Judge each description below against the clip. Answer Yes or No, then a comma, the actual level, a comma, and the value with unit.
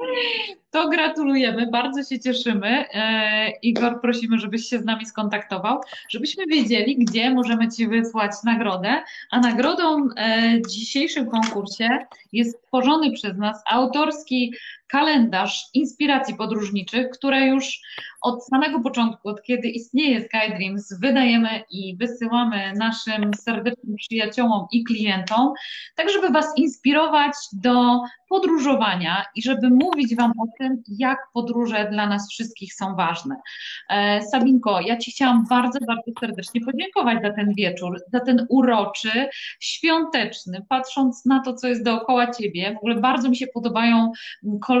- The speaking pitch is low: No, high, 240 Hz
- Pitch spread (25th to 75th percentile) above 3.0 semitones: Yes, average, 3.4 semitones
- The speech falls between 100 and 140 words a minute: Yes, average, 135 wpm